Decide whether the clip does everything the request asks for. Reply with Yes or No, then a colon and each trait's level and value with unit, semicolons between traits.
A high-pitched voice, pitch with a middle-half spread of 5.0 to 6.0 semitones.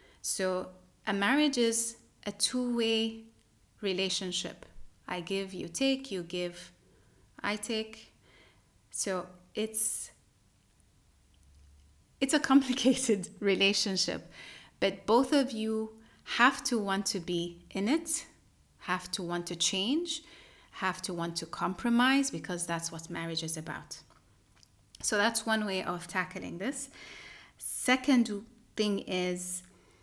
Yes: high, 195 Hz; average, 5.3 semitones